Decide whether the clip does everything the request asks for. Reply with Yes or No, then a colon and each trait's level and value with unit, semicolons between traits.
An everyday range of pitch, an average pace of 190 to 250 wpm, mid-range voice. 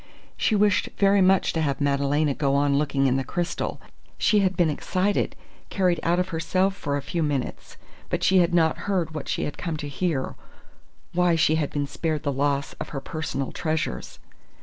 Yes: average, 4.2 semitones; average, 195 wpm; medium, 160 Hz